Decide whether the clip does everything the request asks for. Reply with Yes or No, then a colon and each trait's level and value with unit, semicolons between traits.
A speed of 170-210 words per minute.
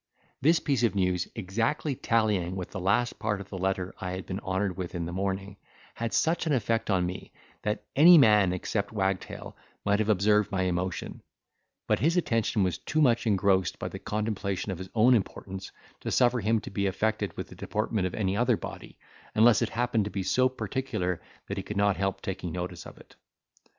Yes: average, 200 wpm